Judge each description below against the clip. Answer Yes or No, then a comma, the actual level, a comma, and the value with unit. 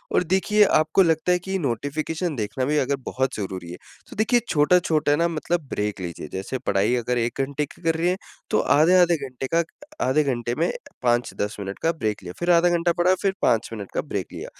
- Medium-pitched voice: Yes, medium, 145 Hz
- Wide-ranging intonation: Yes, wide, 6.4 semitones